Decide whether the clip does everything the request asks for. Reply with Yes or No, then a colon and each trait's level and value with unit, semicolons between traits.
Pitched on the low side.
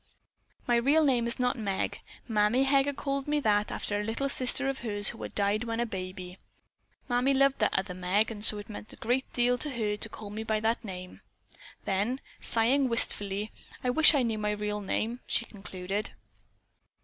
No: high, 225 Hz